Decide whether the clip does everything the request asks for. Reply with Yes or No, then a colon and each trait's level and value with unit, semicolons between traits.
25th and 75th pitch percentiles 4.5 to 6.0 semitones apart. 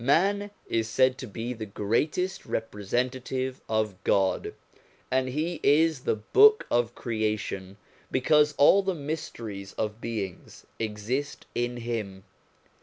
Yes: average, 5.2 semitones